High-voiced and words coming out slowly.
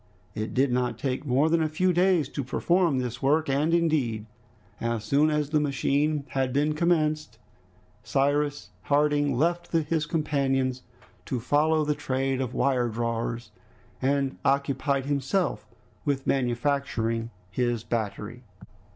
No: medium, 140 Hz; slow, 130 wpm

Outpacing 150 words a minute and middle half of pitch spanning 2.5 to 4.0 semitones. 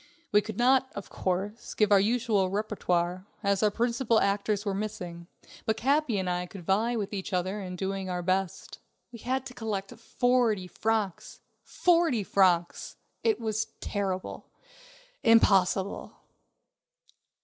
No: average, 140 wpm; average, 3.3 semitones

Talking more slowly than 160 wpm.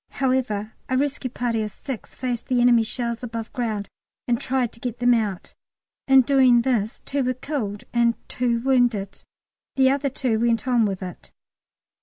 No: average, 170 wpm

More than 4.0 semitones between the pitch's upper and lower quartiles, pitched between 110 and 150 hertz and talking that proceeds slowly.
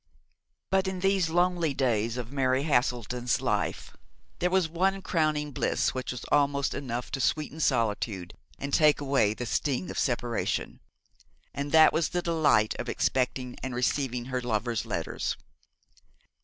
No: average, 4.6 semitones; low, 135 Hz; average, 145 wpm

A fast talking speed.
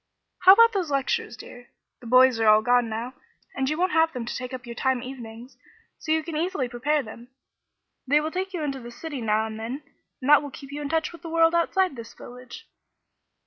Yes: fast, 225 wpm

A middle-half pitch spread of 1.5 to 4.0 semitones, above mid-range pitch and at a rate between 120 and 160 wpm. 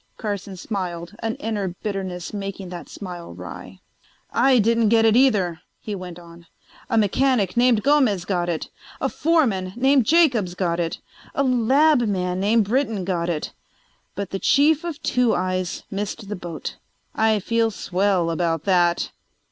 No: average, 4.5 semitones; high, 200 Hz; average, 155 wpm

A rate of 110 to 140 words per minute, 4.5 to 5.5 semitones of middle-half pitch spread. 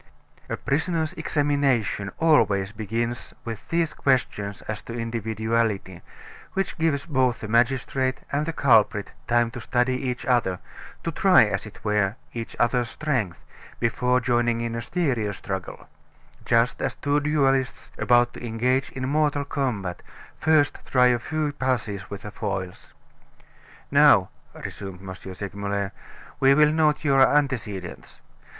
Yes: slow, 135 wpm; average, 4.8 semitones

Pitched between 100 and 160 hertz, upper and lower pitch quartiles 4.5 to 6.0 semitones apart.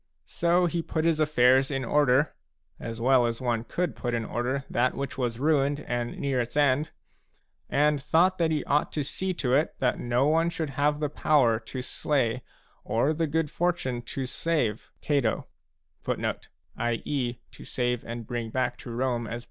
No: medium, 140 Hz; average, 3.9 semitones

